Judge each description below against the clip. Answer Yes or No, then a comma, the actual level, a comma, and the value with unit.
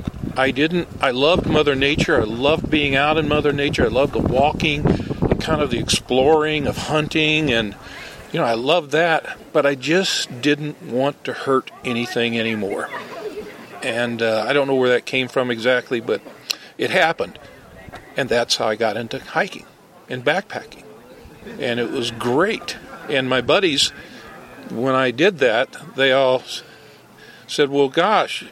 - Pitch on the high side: No, medium, 140 Hz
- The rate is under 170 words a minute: Yes, average, 160 wpm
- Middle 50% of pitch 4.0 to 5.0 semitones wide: No, average, 3.6 semitones